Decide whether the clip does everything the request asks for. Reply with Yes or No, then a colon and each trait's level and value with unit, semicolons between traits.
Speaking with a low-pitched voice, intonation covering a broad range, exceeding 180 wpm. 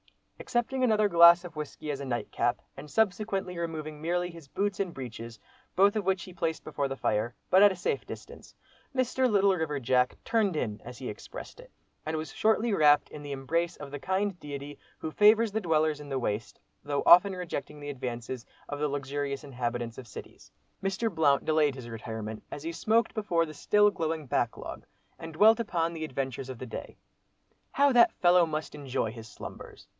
No: medium, 155 Hz; wide, 5.9 semitones; average, 190 wpm